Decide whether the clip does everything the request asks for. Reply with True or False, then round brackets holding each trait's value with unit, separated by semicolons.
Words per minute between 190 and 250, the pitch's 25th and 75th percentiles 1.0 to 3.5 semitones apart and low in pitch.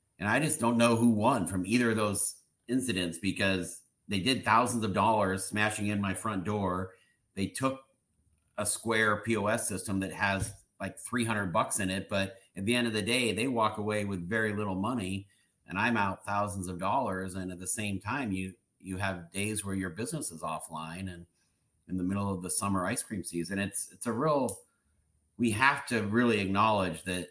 True (200 wpm; 3.1 semitones; 100 Hz)